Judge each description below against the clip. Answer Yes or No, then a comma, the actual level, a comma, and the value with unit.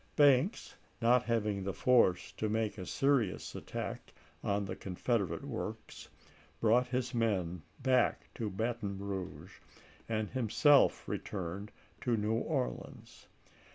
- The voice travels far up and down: No, average, 4.0 semitones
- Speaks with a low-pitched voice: Yes, low, 110 Hz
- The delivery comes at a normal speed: No, slow, 120 wpm